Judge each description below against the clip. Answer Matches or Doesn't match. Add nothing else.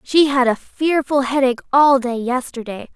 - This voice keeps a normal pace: Matches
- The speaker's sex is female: Matches